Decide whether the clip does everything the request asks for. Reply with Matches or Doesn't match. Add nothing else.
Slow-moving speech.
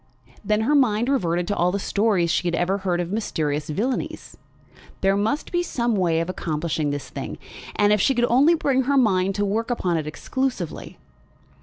Doesn't match